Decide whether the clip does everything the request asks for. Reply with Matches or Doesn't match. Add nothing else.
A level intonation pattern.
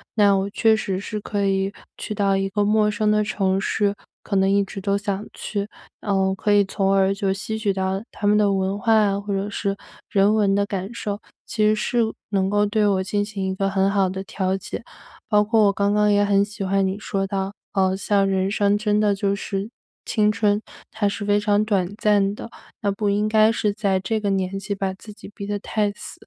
Matches